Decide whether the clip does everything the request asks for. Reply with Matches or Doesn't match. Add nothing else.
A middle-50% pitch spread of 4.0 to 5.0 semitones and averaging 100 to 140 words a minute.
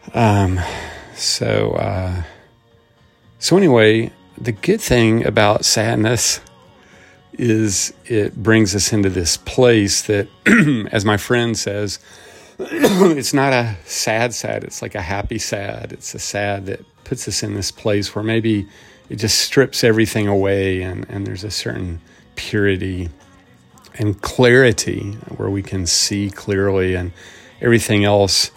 Doesn't match